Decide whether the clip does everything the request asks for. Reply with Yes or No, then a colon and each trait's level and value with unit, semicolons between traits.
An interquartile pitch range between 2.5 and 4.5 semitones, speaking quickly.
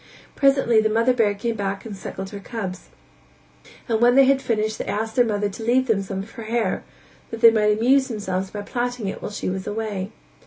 Yes: average, 2.8 semitones; fast, 220 wpm